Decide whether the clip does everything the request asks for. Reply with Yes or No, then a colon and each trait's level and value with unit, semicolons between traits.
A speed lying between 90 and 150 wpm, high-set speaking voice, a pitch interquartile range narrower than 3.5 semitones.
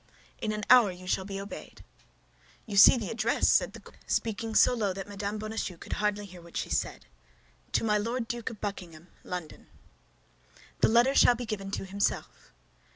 No: average, 185 wpm; high, 210 Hz; narrow, 2.6 semitones